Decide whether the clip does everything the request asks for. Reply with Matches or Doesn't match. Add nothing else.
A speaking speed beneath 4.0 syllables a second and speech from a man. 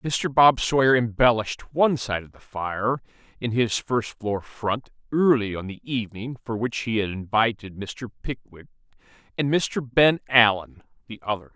Doesn't match